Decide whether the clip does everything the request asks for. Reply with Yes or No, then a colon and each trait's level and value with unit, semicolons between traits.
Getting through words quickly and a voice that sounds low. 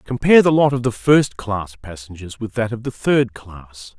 Yes: fast, 210 wpm; low, 115 Hz